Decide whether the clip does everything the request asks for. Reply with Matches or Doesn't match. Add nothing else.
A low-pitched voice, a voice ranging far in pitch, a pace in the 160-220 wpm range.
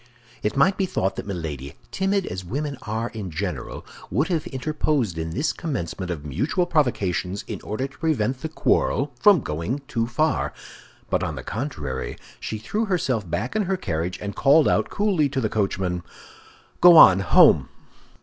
Matches